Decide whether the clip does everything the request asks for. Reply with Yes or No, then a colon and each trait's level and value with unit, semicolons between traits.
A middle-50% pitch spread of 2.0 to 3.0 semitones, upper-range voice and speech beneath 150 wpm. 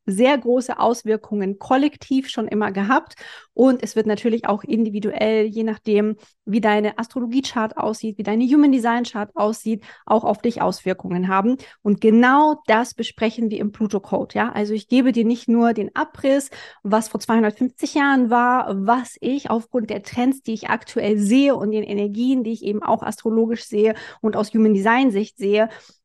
No: average, 2.7 semitones; high, 225 Hz; average, 165 wpm